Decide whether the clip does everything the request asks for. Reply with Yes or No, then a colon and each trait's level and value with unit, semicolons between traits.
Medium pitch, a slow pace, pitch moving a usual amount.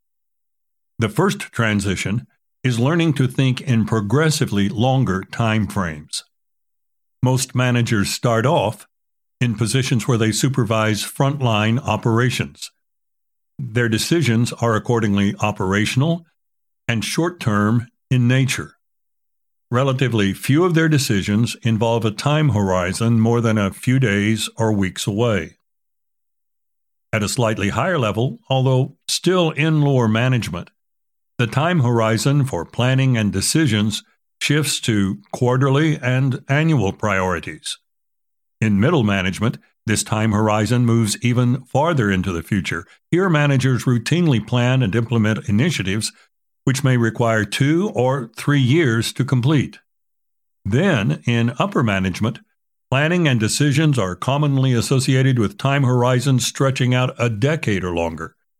No: low, 120 Hz; slow, 125 wpm; average, 3.8 semitones